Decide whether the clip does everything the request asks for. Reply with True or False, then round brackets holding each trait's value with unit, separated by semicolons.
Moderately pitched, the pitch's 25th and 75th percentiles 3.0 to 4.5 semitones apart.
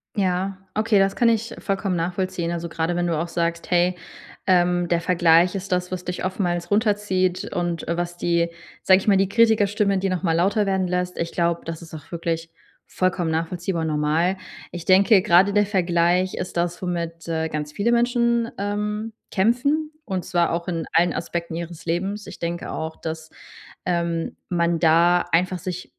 False (180 Hz; 2.5 semitones)